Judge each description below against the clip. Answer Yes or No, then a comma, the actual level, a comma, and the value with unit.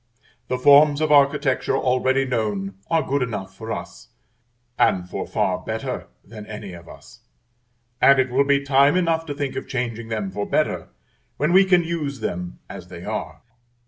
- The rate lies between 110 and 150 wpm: No, average, 175 wpm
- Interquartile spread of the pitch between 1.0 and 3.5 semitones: No, average, 5.1 semitones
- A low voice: Yes, low, 130 Hz